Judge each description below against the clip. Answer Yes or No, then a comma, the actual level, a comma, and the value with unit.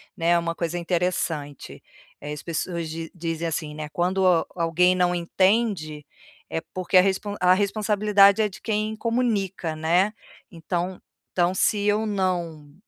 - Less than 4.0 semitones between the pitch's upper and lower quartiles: Yes, average, 3.2 semitones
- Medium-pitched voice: Yes, medium, 180 Hz